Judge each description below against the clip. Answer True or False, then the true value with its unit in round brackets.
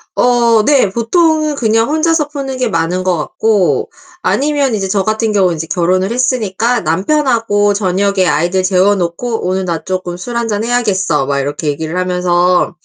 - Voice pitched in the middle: False (200 Hz)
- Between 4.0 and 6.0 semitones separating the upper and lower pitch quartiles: True (5.1 semitones)